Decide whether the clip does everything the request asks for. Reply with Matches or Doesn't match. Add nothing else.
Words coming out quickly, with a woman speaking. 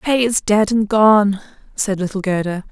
Doesn't match